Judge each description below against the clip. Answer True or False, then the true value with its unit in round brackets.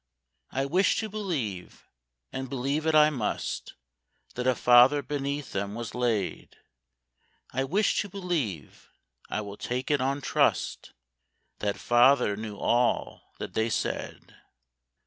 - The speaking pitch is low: True (130 Hz)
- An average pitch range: True (4.9 semitones)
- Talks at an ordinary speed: False (125 wpm)